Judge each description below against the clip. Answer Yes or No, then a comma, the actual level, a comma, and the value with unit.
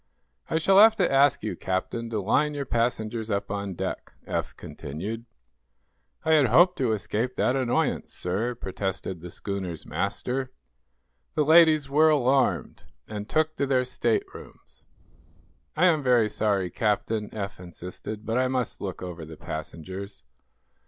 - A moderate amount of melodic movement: No, wide, 5.8 semitones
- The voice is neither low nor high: No, low, 115 Hz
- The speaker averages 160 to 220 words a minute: No, average, 145 wpm